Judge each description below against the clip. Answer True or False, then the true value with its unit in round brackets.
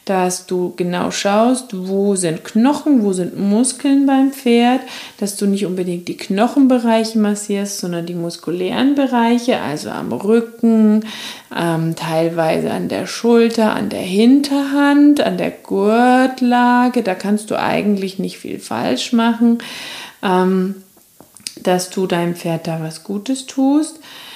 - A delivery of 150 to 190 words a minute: False (130 wpm)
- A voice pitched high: True (220 Hz)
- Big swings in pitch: False (4.8 semitones)